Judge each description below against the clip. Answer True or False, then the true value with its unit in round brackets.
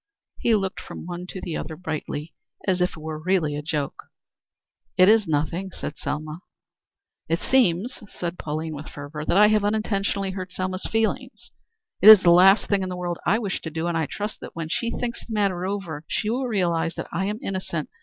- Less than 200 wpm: False (205 wpm)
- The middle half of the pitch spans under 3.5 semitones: False (4.0 semitones)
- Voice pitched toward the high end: False (180 Hz)